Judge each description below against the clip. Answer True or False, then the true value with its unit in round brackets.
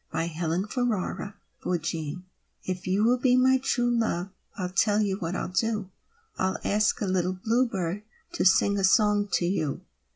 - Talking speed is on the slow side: False (165 wpm)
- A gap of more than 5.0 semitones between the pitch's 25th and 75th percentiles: False (3.5 semitones)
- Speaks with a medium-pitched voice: False (195 Hz)